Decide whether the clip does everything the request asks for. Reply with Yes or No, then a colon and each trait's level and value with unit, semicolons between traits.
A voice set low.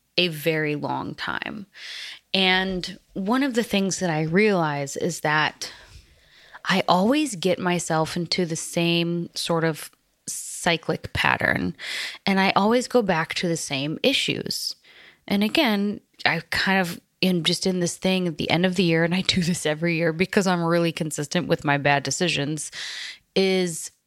No: medium, 175 Hz